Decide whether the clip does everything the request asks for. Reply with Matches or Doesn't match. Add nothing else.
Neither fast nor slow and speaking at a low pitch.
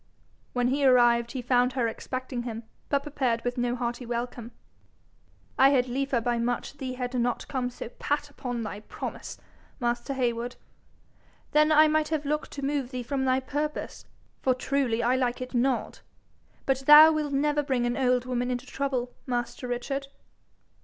Doesn't match